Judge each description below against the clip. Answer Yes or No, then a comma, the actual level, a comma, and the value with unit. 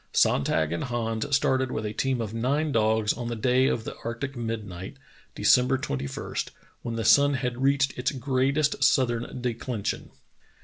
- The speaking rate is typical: Yes, average, 160 wpm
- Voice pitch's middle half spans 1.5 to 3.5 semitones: Yes, average, 3.0 semitones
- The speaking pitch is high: No, low, 120 Hz